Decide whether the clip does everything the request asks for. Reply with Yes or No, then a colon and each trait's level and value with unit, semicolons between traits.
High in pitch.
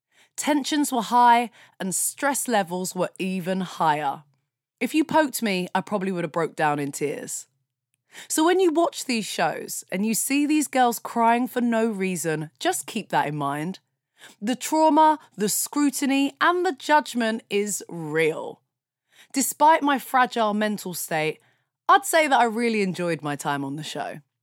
Yes: high, 215 Hz